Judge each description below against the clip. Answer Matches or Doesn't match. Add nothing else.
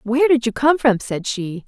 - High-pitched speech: Matches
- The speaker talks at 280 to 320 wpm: Doesn't match